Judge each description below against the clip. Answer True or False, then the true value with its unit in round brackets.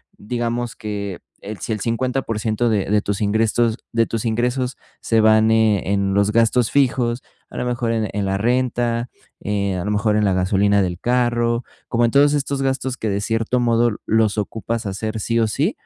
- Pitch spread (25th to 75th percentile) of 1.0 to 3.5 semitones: True (2.5 semitones)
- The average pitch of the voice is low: True (115 Hz)